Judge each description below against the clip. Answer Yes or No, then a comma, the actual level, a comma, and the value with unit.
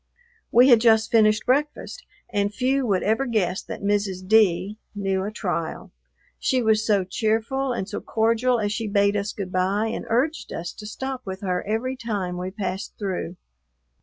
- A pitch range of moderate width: Yes, average, 3.2 semitones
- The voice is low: No, high, 215 Hz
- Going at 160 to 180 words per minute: Yes, average, 175 wpm